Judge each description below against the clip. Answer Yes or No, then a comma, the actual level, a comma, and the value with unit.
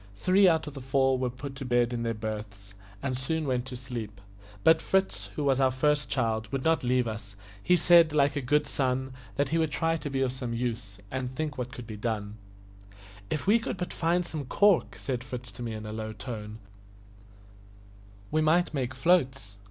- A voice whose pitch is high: No, low, 130 Hz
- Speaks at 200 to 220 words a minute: Yes, fast, 205 wpm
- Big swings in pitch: No, average, 4.5 semitones